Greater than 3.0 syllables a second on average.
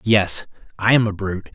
Yes: 5.3 syllables/s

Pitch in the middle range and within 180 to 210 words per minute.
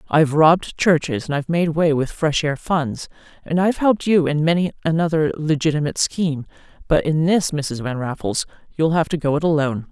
Yes: medium, 155 Hz; average, 195 wpm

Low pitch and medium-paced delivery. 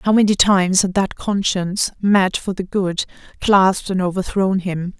No: high, 190 Hz; average, 170 wpm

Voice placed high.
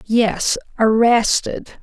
Yes: high, 225 Hz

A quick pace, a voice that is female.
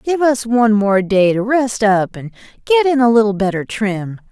Yes: fast, 210 wpm; female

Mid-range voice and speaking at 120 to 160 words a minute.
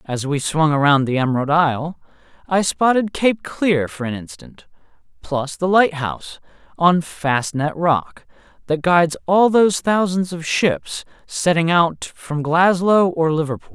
Yes: medium, 155 Hz; average, 145 wpm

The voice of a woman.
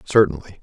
No: male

